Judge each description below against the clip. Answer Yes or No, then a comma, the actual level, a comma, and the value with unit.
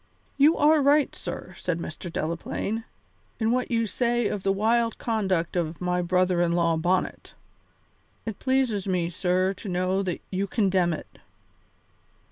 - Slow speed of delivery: No, average, 150 wpm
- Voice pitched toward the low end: No, high, 190 Hz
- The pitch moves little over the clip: No, average, 4.4 semitones